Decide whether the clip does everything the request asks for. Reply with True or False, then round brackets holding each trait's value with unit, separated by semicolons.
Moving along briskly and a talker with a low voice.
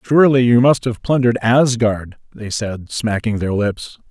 False (160 wpm; 115 Hz)